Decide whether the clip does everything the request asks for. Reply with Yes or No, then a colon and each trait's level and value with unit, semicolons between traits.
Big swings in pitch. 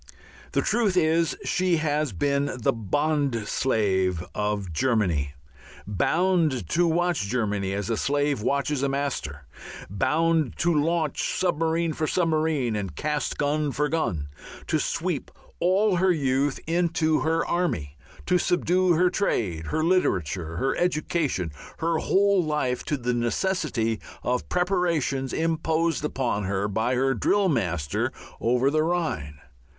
Yes: wide, 7.2 semitones